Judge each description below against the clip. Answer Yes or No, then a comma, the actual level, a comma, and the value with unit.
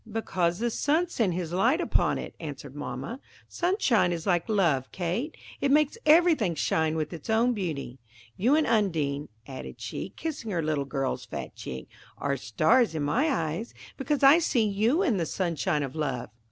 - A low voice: No, medium, 185 Hz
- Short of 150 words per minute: No, average, 170 wpm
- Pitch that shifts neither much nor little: No, wide, 8.6 semitones